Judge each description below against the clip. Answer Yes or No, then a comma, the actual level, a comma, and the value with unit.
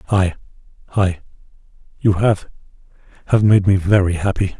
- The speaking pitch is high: No, very low, 95 Hz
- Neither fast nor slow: No, slow, 80 wpm